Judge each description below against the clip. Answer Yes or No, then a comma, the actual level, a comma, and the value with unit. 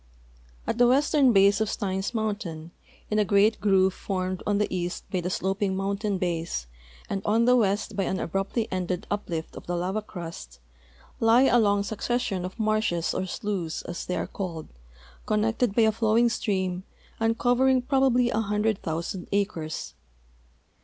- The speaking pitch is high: Yes, high, 200 Hz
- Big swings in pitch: No, average, 3.3 semitones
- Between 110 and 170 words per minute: Yes, average, 160 wpm